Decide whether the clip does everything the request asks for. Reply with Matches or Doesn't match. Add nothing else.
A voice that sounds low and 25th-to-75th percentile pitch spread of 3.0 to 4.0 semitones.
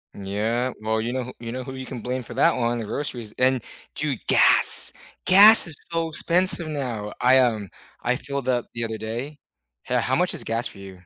Matches